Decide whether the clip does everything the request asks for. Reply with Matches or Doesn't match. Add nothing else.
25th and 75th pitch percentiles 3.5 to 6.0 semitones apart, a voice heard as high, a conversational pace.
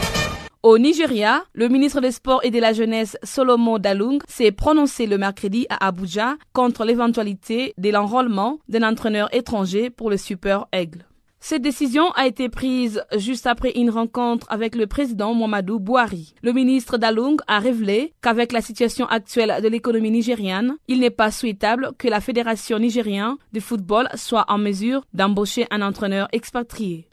Doesn't match